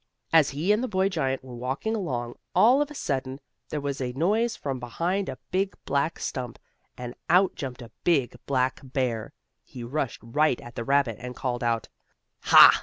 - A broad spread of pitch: Yes, wide, 6.0 semitones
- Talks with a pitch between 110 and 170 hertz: Yes, low, 135 Hz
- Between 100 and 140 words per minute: No, average, 185 wpm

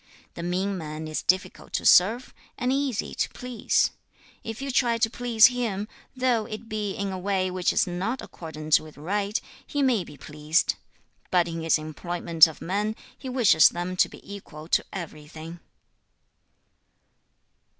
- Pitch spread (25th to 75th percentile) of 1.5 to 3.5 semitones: No, average, 5.3 semitones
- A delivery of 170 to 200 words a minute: No, average, 160 wpm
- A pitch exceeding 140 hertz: Yes, high, 190 Hz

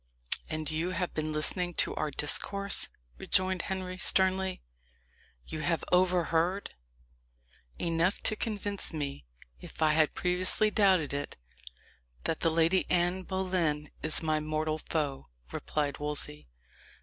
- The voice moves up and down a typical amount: Yes, average, 3.5 semitones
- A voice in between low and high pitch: Yes, medium, 165 Hz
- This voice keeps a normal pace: No, slow, 125 wpm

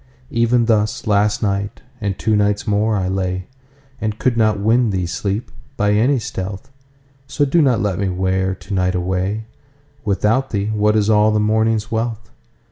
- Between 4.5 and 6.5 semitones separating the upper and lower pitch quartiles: No, average, 3.1 semitones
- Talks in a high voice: No, low, 105 Hz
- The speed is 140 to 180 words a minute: Yes, average, 155 wpm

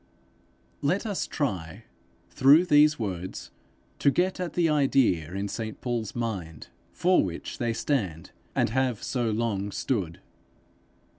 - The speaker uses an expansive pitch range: Yes, wide, 6.8 semitones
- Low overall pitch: Yes, low, 115 Hz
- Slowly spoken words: Yes, slow, 130 wpm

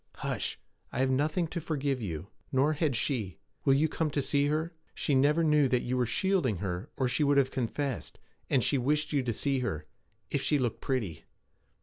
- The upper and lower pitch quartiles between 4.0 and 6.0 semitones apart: No, average, 3.5 semitones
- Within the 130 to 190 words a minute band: No, fast, 205 wpm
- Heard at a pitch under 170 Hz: Yes, low, 135 Hz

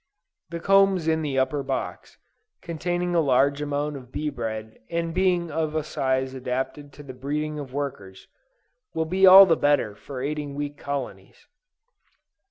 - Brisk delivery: No, average, 160 wpm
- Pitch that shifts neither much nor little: Yes, average, 3.6 semitones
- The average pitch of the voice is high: No, medium, 145 Hz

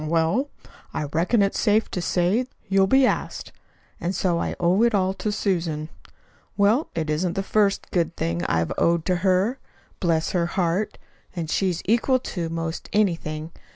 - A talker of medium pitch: Yes, medium, 180 Hz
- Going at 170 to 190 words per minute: Yes, average, 175 wpm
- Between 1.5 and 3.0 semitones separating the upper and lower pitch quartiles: No, average, 3.6 semitones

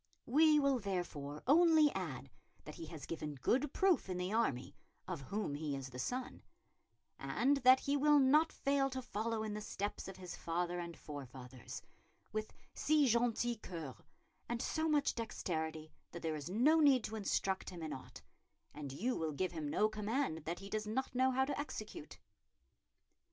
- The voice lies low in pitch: No, high, 210 Hz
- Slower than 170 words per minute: No, average, 180 wpm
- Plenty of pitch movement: Yes, wide, 8.6 semitones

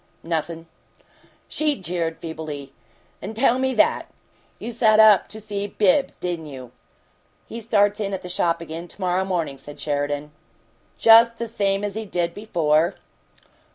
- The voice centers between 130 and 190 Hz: Yes, medium, 185 Hz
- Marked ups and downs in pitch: No, average, 5.0 semitones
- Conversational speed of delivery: Yes, average, 155 wpm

